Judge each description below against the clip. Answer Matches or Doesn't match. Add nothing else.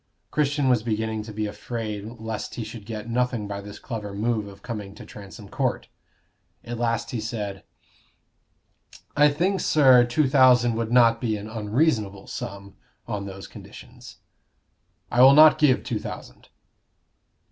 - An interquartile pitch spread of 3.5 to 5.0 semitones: Doesn't match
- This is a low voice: Matches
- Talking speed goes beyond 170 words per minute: Doesn't match